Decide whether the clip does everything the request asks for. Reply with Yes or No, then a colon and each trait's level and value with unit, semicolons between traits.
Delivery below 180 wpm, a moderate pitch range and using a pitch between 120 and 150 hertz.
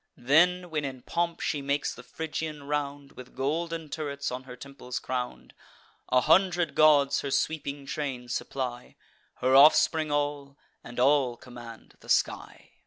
Yes: average, 145 wpm; average, 3.2 semitones; medium, 140 Hz